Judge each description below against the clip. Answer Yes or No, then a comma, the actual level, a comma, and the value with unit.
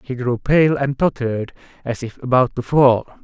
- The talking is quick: No, average, 185 wpm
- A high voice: No, low, 130 Hz